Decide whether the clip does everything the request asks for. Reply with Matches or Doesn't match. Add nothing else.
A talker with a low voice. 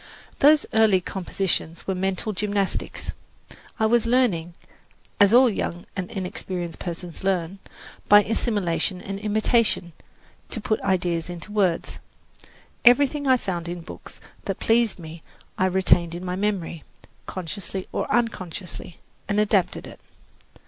Doesn't match